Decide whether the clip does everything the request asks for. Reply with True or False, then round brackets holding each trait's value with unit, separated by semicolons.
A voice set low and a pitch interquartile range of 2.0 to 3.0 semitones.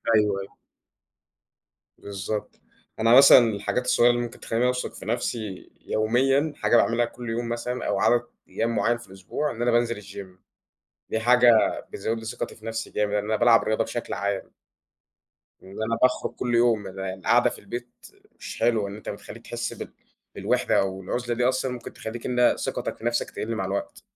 True (115 Hz; 2.6 semitones)